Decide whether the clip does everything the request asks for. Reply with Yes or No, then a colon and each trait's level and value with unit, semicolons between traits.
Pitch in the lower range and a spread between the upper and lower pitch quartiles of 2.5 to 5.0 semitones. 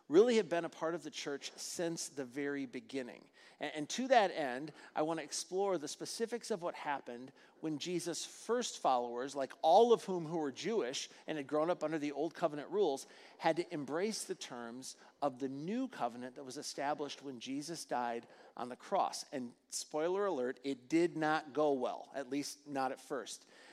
No: medium, 150 Hz; average, 4.1 semitones